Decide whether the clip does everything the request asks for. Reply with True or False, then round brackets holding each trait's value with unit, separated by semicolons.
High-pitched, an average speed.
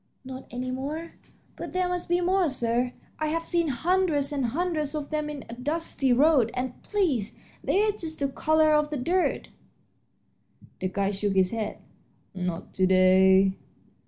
True (285 Hz; 160 wpm)